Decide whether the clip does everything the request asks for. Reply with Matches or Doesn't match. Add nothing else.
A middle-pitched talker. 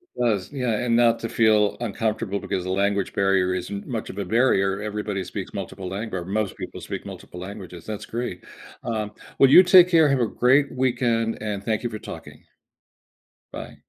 Doesn't match